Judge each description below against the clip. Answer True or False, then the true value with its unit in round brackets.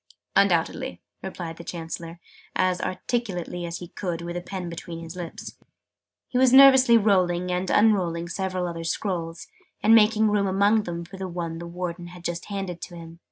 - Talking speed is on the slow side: False (175 wpm)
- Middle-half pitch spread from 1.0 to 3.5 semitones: True (2.8 semitones)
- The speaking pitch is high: False (180 Hz)